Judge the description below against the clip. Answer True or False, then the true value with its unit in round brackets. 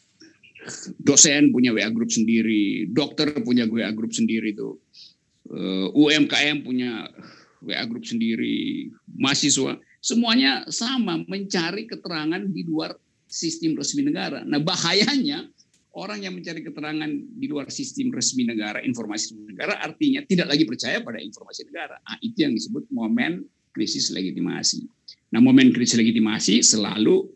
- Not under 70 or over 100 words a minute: False (130 wpm)